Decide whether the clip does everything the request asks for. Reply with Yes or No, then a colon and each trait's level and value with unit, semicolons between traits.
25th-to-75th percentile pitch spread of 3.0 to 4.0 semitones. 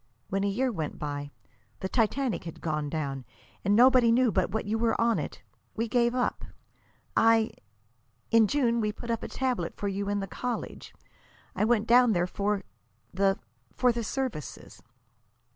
Yes: average, 3.6 semitones